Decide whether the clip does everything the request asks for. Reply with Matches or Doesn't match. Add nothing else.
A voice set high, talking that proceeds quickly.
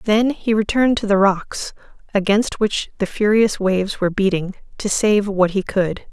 Doesn't match